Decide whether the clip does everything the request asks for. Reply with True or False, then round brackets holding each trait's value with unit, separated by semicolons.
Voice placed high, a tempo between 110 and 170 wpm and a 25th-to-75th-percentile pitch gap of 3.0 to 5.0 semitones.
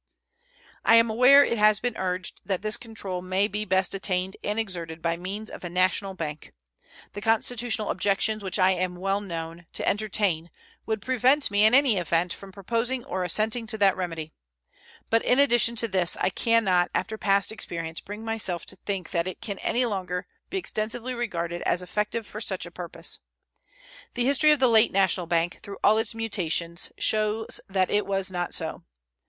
False (200 Hz; 185 wpm; 3.7 semitones)